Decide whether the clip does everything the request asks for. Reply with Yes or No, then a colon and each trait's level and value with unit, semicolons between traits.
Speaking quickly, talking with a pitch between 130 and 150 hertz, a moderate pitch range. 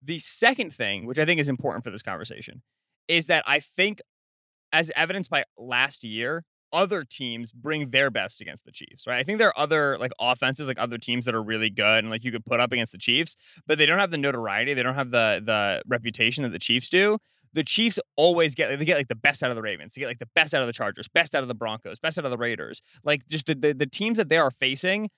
No: fast, 260 wpm; medium, 140 Hz; wide, 5.7 semitones